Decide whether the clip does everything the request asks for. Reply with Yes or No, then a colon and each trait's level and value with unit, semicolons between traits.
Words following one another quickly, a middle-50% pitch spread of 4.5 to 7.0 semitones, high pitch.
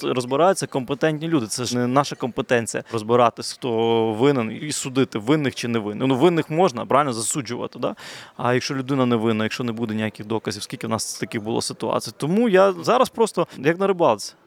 No: fast, 190 wpm; average, 4.8 semitones; low, 130 Hz